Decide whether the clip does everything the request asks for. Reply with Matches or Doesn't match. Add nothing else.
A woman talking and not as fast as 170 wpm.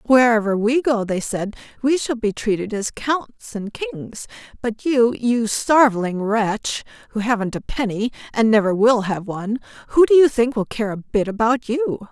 Doesn't match